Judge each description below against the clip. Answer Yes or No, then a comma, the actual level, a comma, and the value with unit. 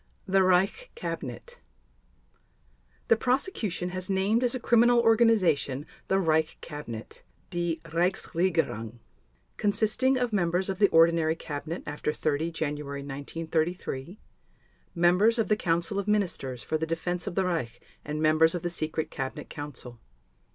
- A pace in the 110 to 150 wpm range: Yes, slow, 135 wpm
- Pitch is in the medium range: Yes, medium, 170 Hz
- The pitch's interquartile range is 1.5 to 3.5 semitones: No, average, 4.5 semitones